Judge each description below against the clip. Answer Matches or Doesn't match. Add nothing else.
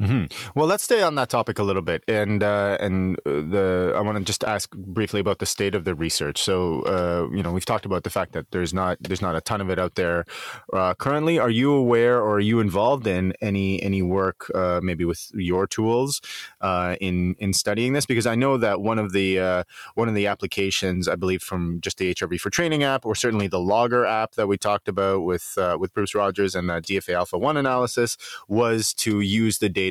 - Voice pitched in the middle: Doesn't match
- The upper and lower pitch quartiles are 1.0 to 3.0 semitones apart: Doesn't match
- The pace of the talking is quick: Matches